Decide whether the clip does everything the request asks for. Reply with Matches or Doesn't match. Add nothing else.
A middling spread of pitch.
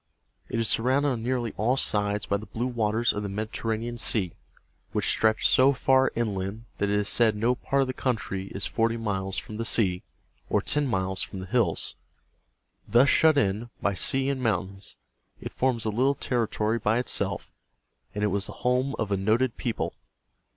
Matches